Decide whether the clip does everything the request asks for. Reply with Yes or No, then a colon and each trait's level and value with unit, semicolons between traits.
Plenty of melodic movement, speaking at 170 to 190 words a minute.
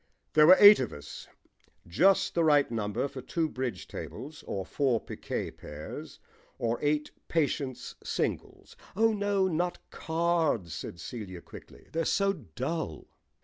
No: wide, 7.0 semitones; average, 140 wpm